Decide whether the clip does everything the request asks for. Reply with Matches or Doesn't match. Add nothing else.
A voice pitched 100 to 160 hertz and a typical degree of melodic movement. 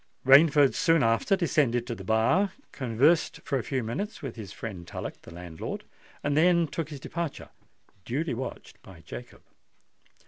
Doesn't match